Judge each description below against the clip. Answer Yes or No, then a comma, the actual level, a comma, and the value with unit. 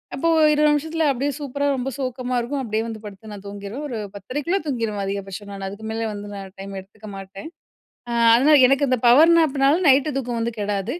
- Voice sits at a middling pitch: No, high, 235 Hz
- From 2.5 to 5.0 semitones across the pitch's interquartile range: No, wide, 5.5 semitones